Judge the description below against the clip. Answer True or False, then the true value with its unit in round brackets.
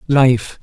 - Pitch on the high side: False (125 Hz)